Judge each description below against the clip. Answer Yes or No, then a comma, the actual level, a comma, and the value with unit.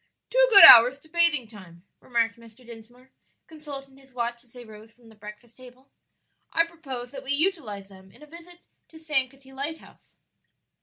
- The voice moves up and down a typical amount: Yes, average, 4.6 semitones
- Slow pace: No, average, 170 wpm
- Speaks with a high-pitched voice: Yes, very high, 255 Hz